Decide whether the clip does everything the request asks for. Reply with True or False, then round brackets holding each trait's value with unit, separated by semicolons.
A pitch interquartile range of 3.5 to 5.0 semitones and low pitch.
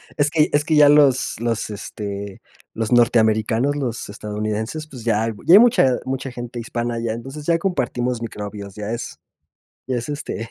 True (4.5 semitones; 120 Hz)